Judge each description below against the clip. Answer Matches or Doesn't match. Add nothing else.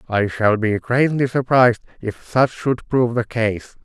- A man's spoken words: Matches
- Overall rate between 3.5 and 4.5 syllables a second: Matches